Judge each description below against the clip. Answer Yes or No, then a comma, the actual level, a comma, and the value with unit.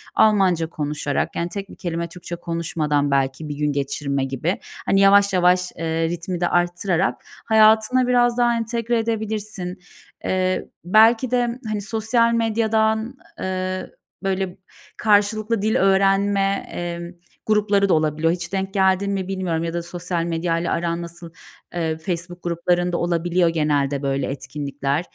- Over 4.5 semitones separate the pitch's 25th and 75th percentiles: No, average, 3.9 semitones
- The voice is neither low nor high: Yes, medium, 180 Hz